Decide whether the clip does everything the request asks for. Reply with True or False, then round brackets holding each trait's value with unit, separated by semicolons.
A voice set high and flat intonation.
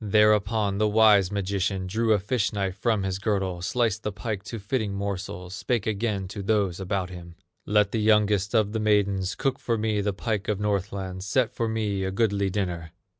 False (100 Hz; 2.0 semitones)